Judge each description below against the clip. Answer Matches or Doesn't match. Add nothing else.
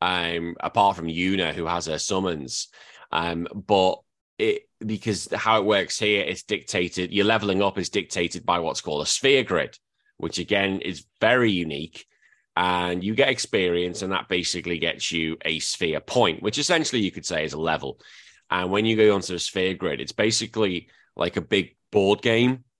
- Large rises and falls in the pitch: Doesn't match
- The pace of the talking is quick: Doesn't match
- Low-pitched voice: Matches